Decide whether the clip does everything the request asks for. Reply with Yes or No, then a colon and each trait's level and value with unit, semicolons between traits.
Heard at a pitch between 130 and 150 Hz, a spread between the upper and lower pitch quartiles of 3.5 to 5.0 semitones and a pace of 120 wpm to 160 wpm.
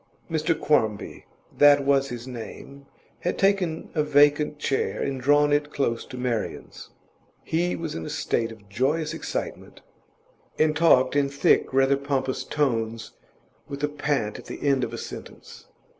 No: medium, 140 Hz; average, 2.8 semitones; average, 155 wpm